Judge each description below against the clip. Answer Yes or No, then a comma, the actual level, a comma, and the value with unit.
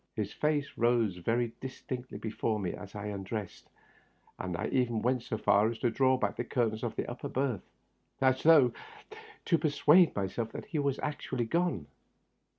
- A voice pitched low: Yes, low, 120 Hz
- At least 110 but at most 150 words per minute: No, average, 175 wpm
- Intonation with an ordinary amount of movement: Yes, average, 3.7 semitones